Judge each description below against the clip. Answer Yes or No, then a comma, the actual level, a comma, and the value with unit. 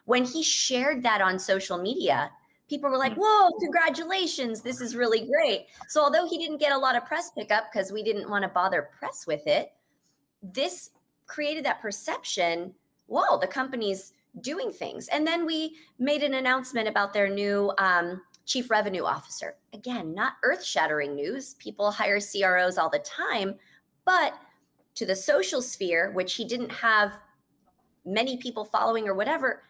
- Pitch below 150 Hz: No, high, 225 Hz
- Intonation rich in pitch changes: Yes, wide, 6.6 semitones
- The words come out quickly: No, average, 165 wpm